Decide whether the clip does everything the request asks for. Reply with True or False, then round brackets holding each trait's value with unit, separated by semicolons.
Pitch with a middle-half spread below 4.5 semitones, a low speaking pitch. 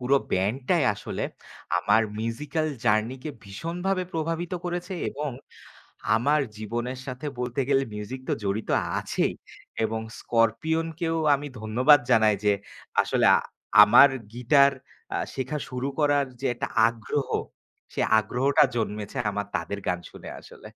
False (5.1 semitones; 125 Hz)